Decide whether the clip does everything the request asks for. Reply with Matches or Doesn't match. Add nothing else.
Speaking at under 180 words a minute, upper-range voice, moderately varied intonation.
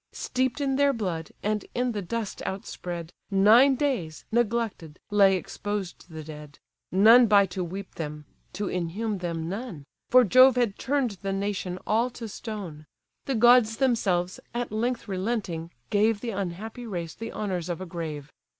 Matches